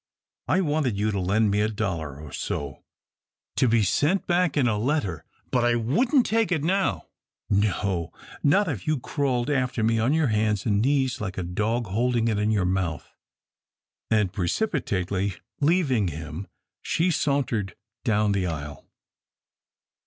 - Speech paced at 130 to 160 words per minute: Yes, average, 155 wpm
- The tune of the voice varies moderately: No, wide, 6.6 semitones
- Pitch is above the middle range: No, low, 110 Hz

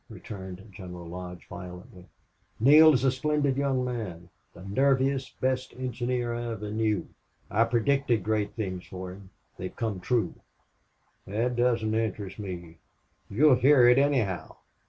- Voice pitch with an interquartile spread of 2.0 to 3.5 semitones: No, average, 5.3 semitones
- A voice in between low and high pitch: No, low, 115 Hz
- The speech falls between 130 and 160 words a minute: Yes, average, 140 wpm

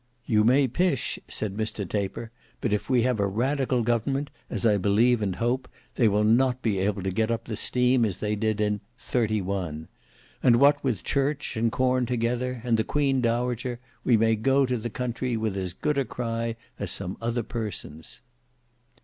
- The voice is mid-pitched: No, low, 115 Hz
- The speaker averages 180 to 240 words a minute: Yes, average, 185 wpm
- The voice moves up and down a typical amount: Yes, average, 3.1 semitones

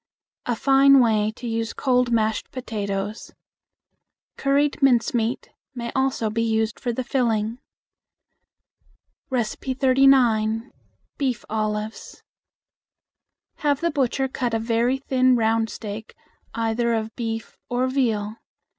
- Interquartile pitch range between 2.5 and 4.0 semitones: Yes, average, 2.8 semitones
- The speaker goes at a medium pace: No, slow, 105 wpm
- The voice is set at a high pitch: Yes, high, 235 Hz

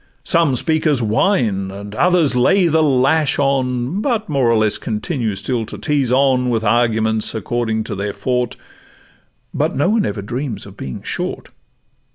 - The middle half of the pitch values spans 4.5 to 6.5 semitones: Yes, average, 5.1 semitones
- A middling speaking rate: Yes, average, 160 wpm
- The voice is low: Yes, low, 125 Hz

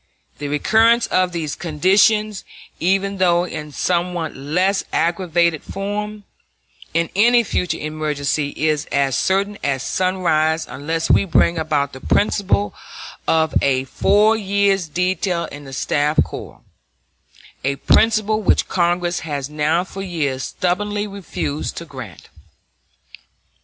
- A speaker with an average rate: No, slow, 120 wpm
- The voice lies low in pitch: No, medium, 170 Hz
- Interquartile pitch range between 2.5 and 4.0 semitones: No, average, 4.7 semitones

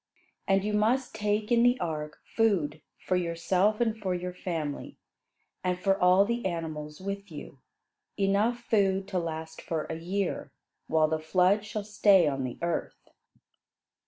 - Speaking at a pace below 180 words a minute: Yes, average, 150 wpm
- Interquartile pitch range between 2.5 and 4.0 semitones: No, average, 4.4 semitones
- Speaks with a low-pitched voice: No, medium, 185 Hz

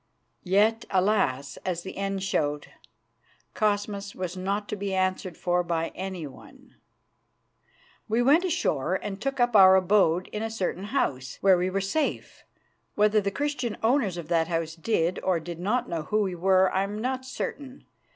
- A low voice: No, high, 195 Hz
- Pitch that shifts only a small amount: No, average, 3.6 semitones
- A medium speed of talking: Yes, average, 165 wpm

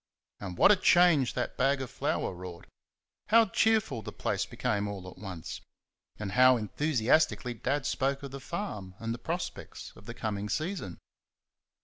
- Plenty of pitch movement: Yes, wide, 7.4 semitones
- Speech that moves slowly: No, average, 160 wpm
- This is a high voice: No, low, 125 Hz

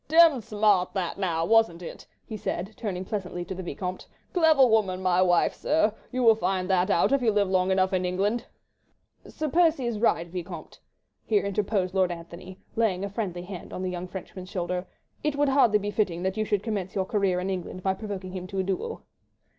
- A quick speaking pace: Yes, fast, 210 wpm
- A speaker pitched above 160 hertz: Yes, high, 190 Hz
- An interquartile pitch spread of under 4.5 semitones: Yes, average, 3.2 semitones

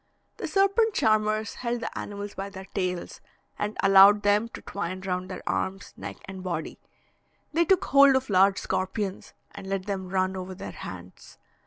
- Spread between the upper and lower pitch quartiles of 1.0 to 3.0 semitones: Yes, narrow, 2.4 semitones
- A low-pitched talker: No, high, 195 Hz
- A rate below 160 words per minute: No, average, 170 wpm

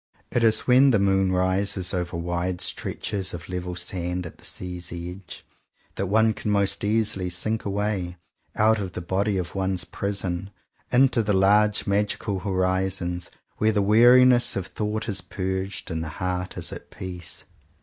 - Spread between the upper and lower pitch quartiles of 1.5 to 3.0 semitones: Yes, average, 2.7 semitones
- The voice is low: Yes, very low, 95 Hz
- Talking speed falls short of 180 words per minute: Yes, average, 160 wpm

